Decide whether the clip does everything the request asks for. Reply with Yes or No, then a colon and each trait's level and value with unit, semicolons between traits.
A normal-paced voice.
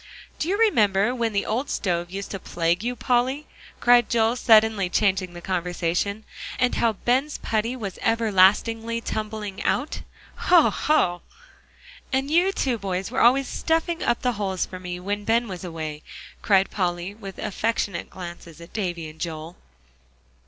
Yes: average, 155 wpm